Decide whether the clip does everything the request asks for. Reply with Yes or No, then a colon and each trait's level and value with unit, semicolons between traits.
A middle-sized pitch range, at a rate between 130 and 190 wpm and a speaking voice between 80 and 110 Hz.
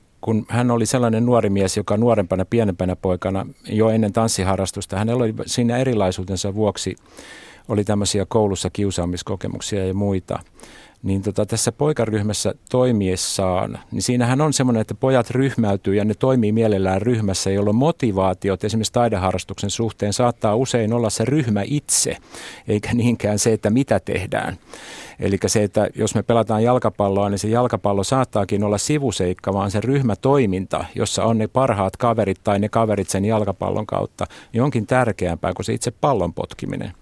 Yes: average, 3.2 semitones; average, 150 wpm; low, 105 Hz